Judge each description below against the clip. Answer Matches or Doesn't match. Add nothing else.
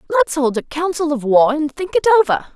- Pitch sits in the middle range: Doesn't match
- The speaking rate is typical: Doesn't match